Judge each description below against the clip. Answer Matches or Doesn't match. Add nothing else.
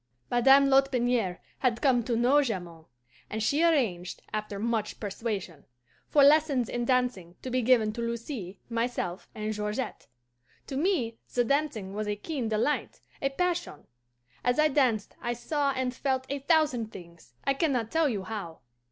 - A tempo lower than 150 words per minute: Doesn't match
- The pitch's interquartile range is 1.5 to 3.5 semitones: Doesn't match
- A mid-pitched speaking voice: Doesn't match